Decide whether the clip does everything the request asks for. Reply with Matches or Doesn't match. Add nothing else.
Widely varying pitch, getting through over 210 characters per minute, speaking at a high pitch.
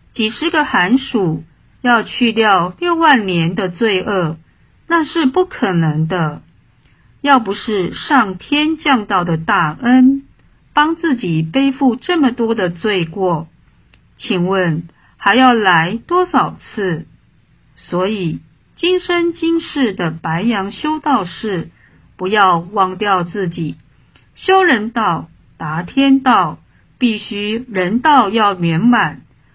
Doesn't match